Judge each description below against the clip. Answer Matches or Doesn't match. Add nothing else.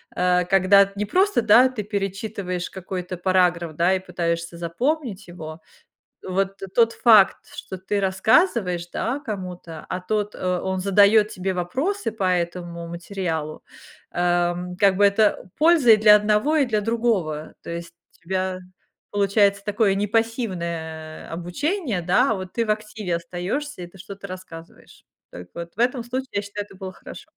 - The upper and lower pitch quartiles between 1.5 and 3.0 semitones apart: Doesn't match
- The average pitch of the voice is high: Matches